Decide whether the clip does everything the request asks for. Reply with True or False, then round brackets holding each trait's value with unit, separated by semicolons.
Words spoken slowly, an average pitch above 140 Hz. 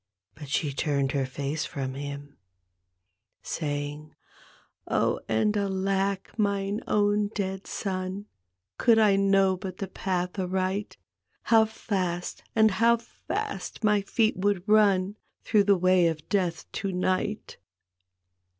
True (130 wpm; 190 Hz)